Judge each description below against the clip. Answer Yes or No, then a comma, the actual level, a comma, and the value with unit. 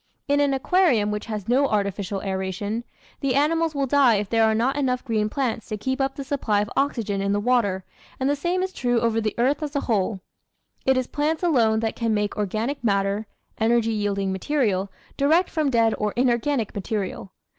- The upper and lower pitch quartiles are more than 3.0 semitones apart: Yes, average, 4.9 semitones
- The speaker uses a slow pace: No, average, 200 wpm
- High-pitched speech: Yes, high, 230 Hz